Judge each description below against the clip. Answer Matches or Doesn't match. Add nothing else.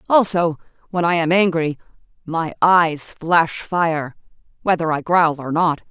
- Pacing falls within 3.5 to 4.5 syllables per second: Matches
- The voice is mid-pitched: Matches